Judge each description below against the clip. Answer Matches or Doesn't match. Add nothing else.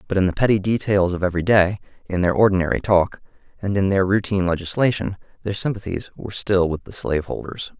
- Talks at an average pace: Matches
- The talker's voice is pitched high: Doesn't match